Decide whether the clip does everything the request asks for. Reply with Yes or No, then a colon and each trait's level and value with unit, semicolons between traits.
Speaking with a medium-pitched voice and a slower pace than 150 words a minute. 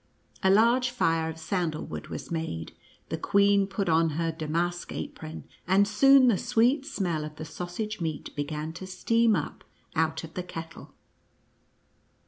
No: medium, 175 Hz; average, 155 wpm